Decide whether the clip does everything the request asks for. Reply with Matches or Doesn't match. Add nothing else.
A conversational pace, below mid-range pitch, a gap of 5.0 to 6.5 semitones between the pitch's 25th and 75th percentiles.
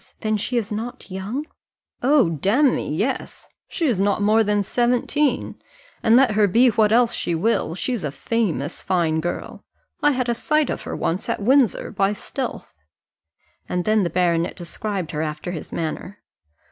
Doesn't match